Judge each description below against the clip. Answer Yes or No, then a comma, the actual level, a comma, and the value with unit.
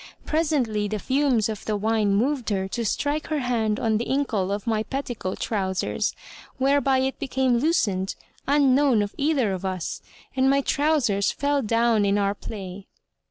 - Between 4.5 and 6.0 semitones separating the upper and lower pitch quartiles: Yes, average, 5.1 semitones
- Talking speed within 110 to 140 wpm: No, average, 160 wpm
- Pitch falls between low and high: No, high, 230 Hz